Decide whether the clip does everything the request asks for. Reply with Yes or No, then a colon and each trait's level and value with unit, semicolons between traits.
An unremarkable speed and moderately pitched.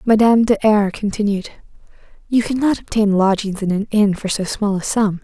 No: average, 185 wpm; high, 210 Hz